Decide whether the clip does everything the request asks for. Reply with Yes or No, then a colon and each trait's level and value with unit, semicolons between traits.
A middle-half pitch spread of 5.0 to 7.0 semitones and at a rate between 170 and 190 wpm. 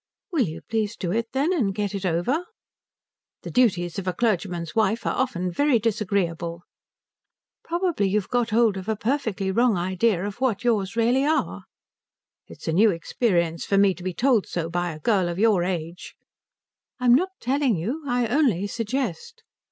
Yes: average, 5.3 semitones; average, 180 wpm